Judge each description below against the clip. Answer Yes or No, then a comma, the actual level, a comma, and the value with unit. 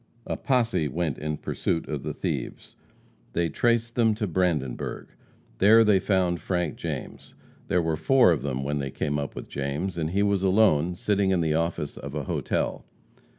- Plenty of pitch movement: No, average, 5.0 semitones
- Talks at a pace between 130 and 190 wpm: Yes, average, 180 wpm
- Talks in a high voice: No, very low, 85 Hz